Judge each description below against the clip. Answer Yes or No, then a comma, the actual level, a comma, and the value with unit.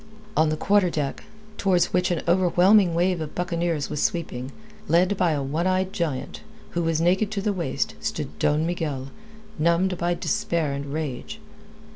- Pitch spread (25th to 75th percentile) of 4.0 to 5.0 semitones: No, average, 3.1 semitones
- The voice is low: No, medium, 170 Hz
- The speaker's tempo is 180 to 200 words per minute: No, average, 165 wpm